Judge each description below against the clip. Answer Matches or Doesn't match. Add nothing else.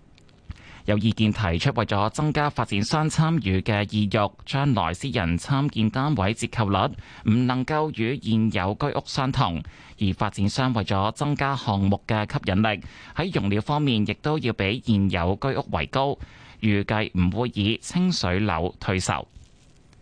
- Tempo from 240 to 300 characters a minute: Doesn't match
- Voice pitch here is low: Matches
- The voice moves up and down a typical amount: Matches